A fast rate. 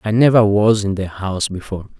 Yes: fast, 210 wpm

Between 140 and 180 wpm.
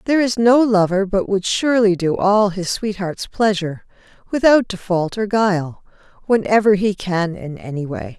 Yes: average, 170 wpm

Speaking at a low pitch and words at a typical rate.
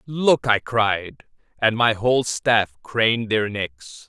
Yes: low, 110 Hz; average, 145 wpm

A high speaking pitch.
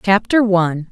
Yes: high, 195 Hz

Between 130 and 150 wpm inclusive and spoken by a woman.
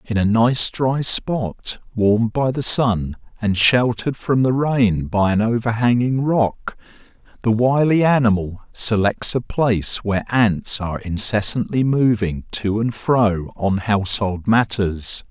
No: slow, 135 wpm; male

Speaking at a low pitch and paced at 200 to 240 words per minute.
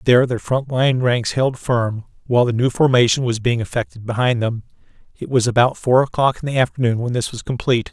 Yes: low, 120 Hz; fast, 205 wpm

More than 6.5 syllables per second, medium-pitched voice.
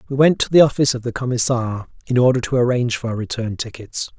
No: 6.7 syllables/s; low, 125 Hz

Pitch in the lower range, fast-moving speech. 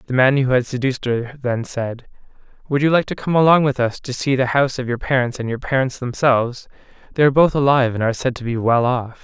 Yes: low, 130 Hz; fast, 245 wpm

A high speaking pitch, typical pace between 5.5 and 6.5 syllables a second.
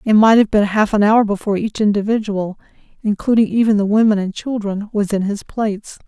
Yes: high, 210 Hz; 5.7 syllables/s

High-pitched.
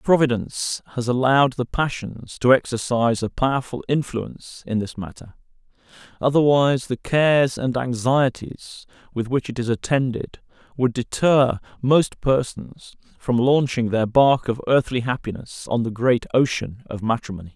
No: low, 125 Hz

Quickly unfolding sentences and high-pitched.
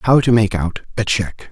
No: fast, 240 wpm; low, 105 Hz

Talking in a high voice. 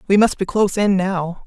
Yes: high, 195 Hz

